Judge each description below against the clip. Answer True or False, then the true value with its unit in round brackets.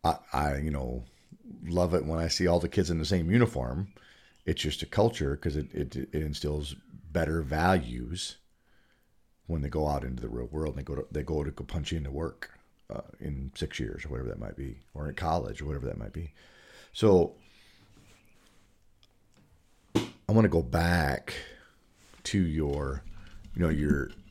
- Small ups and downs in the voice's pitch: False (4.3 semitones)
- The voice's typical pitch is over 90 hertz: False (80 Hz)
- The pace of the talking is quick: False (180 wpm)